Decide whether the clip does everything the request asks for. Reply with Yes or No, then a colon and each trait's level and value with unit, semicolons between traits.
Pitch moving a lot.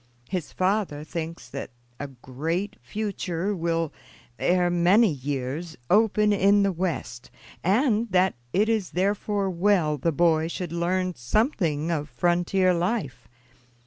No: average, 4.0 semitones